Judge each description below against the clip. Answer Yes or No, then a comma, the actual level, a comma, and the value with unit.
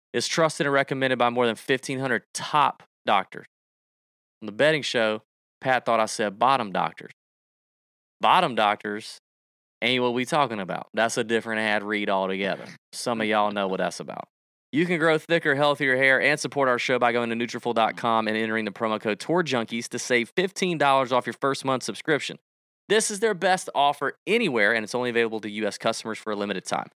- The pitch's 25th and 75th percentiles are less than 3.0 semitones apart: No, average, 4.1 semitones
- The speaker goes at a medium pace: Yes, average, 190 wpm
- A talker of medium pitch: No, low, 120 Hz